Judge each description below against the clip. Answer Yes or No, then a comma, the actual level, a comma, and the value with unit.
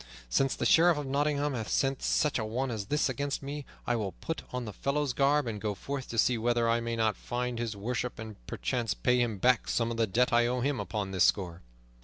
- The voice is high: No, low, 120 Hz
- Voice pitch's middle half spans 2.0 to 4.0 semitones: Yes, average, 3.6 semitones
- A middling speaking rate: No, fast, 240 wpm